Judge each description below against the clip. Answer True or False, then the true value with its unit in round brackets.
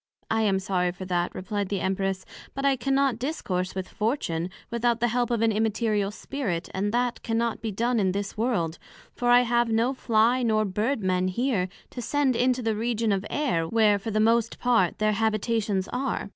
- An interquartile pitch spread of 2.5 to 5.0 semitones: True (3.9 semitones)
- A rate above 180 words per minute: True (200 wpm)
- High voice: True (220 Hz)